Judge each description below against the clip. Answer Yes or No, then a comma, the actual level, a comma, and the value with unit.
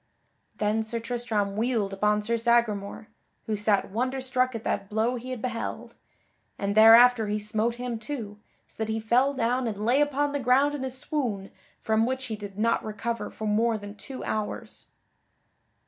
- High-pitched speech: Yes, high, 225 Hz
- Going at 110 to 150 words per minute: No, average, 180 wpm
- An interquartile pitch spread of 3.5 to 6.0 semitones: No, average, 2.9 semitones